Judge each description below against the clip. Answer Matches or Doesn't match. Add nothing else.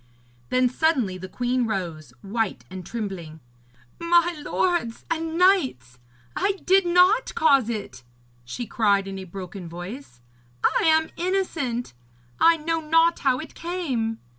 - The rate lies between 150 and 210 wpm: Doesn't match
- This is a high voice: Matches